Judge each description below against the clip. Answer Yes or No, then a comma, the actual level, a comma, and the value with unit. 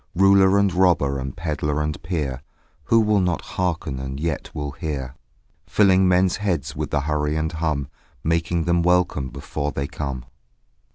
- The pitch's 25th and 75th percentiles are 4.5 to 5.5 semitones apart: No, average, 4.0 semitones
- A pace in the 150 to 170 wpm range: Yes, average, 160 wpm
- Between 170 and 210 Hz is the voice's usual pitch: No, very low, 80 Hz